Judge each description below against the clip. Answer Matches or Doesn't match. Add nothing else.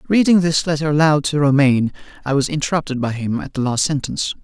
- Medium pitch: Matches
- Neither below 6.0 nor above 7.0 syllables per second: Matches